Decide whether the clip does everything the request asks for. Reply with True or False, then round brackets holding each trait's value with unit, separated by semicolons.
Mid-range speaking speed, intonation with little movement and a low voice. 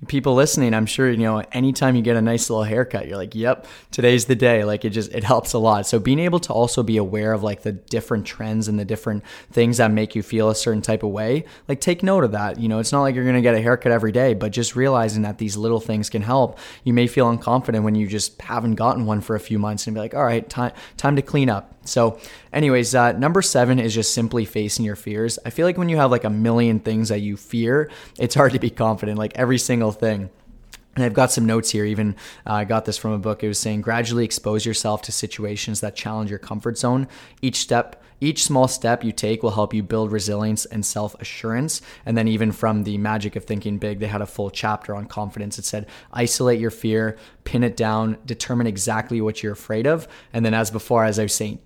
False (250 wpm; 2.3 semitones; 115 Hz)